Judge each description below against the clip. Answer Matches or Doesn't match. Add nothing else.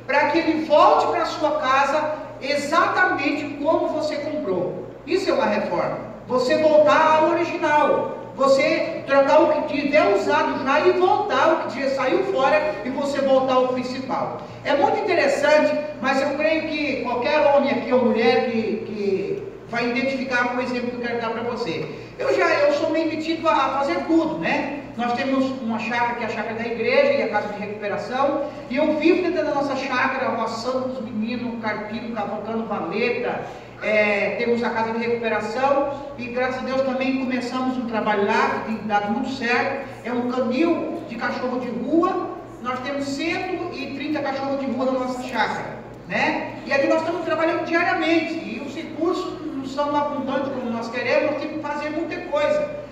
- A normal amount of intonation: Matches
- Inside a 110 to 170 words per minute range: Doesn't match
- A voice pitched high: Matches